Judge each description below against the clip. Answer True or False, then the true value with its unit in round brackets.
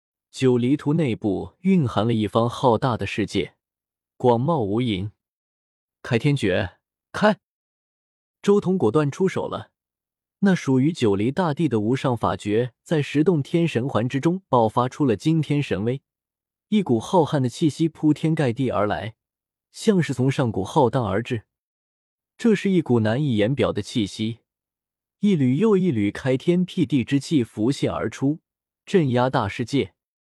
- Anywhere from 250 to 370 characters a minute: False (220 characters per minute)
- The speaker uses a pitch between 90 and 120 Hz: False (135 Hz)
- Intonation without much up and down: False (5.8 semitones)